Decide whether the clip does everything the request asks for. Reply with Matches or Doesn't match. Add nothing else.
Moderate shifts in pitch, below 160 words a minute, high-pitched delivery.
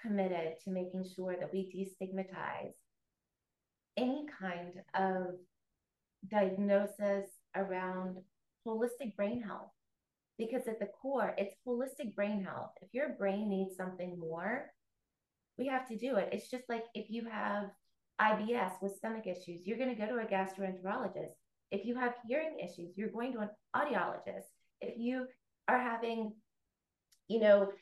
Matches